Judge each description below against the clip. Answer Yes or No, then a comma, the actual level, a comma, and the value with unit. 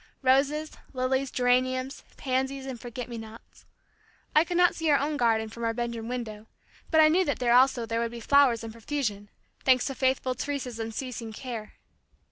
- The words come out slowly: No, average, 180 wpm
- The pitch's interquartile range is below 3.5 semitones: Yes, average, 2.9 semitones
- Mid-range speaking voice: No, very high, 255 Hz